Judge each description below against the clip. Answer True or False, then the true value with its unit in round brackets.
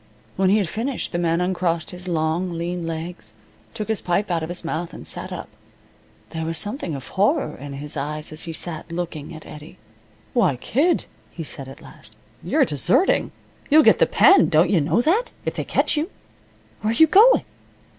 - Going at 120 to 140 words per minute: False (195 wpm)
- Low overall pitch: False (175 Hz)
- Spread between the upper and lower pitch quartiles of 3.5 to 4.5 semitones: False (4.9 semitones)